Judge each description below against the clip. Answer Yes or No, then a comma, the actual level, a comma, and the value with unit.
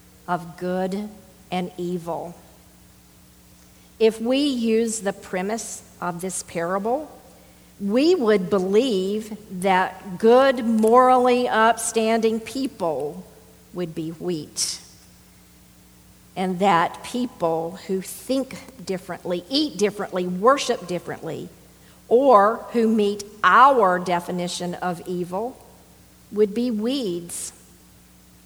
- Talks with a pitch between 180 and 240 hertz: Yes, high, 190 Hz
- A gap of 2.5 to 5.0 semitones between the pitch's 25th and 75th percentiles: Yes, average, 4.5 semitones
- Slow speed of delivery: Yes, slow, 90 wpm